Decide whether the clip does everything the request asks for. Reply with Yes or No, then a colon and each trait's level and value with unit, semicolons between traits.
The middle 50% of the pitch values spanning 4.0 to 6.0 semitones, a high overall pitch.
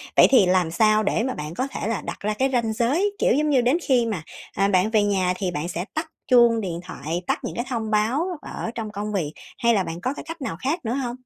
Yes: average, 5.3 semitones; high, 220 Hz